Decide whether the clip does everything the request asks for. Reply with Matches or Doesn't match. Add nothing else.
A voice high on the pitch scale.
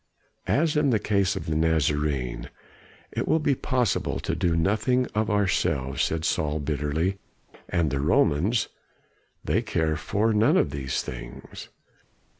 Doesn't match